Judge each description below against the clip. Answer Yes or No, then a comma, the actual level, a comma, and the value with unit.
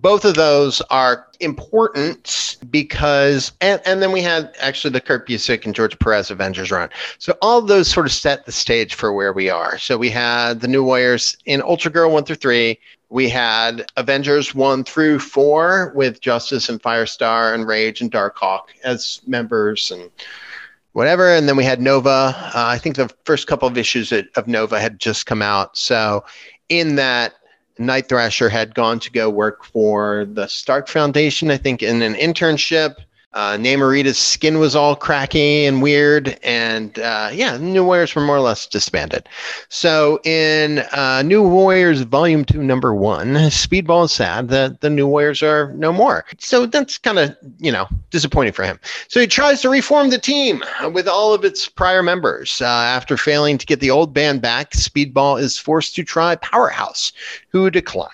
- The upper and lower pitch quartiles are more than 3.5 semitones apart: Yes, average, 5.3 semitones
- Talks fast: No, average, 185 wpm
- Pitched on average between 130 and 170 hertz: Yes, medium, 140 Hz